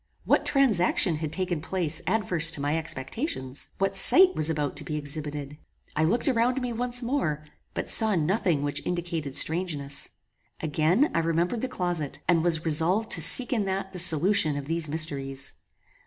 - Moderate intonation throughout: Yes, average, 4.5 semitones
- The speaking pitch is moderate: Yes, medium, 165 Hz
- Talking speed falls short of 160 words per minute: No, average, 170 wpm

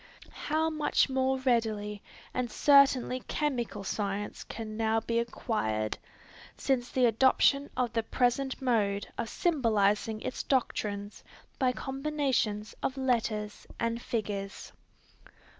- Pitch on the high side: Yes, high, 235 Hz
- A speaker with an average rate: No, slow, 110 wpm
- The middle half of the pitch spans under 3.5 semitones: No, average, 3.9 semitones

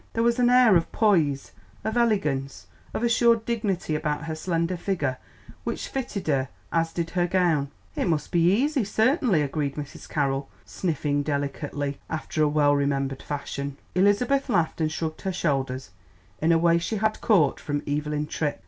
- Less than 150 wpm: No, average, 165 wpm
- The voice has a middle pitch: Yes, medium, 165 Hz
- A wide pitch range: Yes, wide, 5.9 semitones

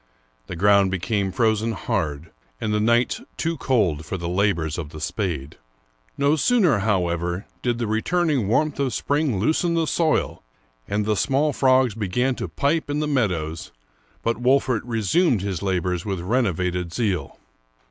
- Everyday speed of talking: Yes, average, 155 wpm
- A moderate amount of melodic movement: No, wide, 6.6 semitones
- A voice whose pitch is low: Yes, low, 105 Hz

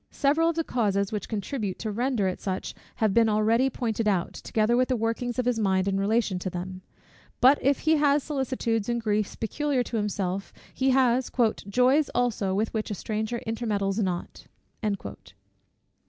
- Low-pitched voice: No, high, 225 Hz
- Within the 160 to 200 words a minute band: Yes, average, 170 wpm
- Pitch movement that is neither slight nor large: Yes, average, 4.0 semitones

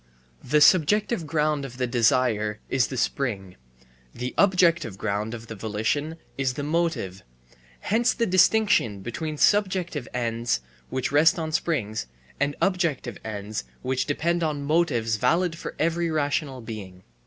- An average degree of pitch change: No, wide, 6.5 semitones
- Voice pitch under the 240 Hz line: Yes, medium, 140 Hz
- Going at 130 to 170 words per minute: Yes, average, 140 wpm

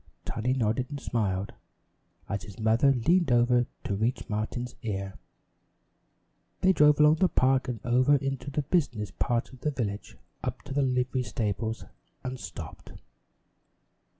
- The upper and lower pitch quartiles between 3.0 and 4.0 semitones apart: Yes, average, 3.7 semitones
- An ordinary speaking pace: Yes, average, 145 wpm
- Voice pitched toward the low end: Yes, low, 125 Hz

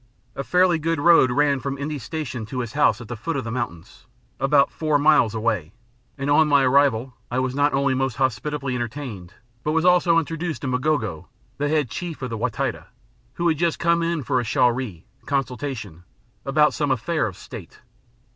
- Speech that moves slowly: No, average, 195 wpm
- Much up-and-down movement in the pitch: No, average, 3.9 semitones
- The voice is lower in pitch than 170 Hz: Yes, medium, 140 Hz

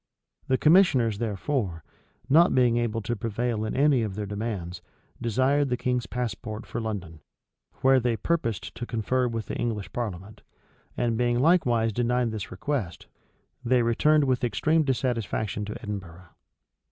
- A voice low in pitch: Yes, low, 120 Hz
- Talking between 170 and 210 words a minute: No, average, 145 wpm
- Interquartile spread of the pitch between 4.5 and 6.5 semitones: No, average, 3.3 semitones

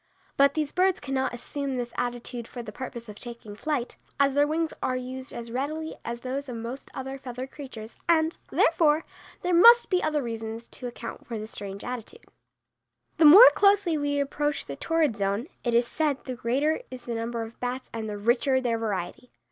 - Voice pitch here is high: Yes, very high, 255 Hz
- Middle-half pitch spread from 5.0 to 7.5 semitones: No, average, 4.1 semitones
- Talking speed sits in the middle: Yes, average, 195 wpm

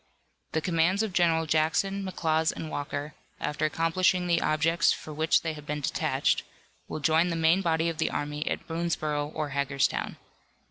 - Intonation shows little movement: Yes, narrow, 1.9 semitones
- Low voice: No, medium, 160 Hz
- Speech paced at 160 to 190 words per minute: Yes, average, 170 wpm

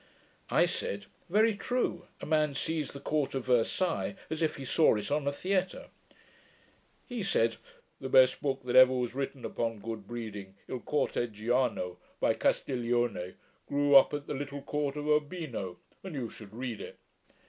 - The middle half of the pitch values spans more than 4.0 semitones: Yes, average, 4.5 semitones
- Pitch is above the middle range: No, low, 135 Hz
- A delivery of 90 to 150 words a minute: No, average, 165 wpm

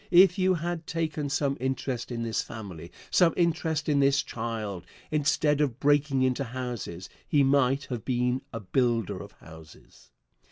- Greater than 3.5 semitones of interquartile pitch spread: Yes, average, 4.5 semitones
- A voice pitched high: No, low, 135 Hz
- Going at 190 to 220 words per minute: No, average, 155 wpm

